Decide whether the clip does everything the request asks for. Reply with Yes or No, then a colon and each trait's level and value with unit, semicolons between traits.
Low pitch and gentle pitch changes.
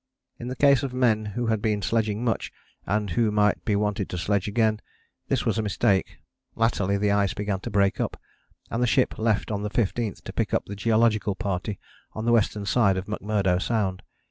Yes: low, 105 Hz; narrow, 2.2 semitones